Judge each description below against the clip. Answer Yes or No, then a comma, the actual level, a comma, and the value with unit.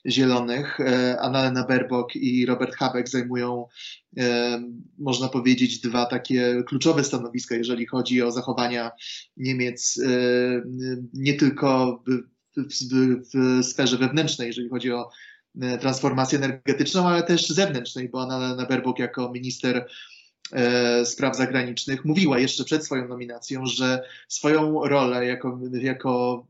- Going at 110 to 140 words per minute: Yes, average, 115 wpm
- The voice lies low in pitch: Yes, low, 125 Hz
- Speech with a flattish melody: Yes, narrow, 1.2 semitones